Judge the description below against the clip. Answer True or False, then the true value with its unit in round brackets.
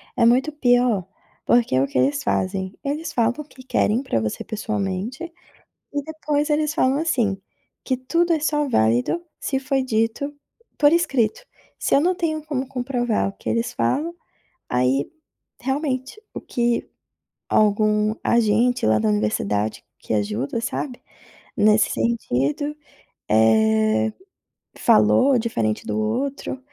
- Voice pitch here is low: False (235 Hz)